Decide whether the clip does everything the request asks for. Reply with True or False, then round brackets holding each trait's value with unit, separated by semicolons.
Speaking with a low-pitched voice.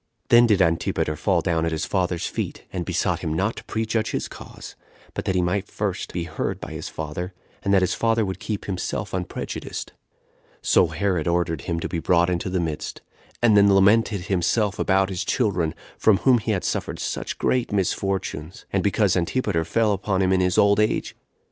True (95 Hz)